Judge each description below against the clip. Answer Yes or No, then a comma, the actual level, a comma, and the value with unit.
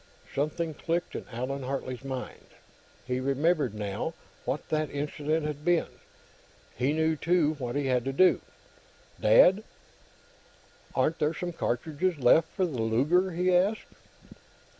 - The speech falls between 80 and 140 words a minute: Yes, slow, 135 wpm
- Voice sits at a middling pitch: Yes, medium, 150 Hz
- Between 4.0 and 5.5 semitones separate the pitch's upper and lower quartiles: Yes, average, 4.5 semitones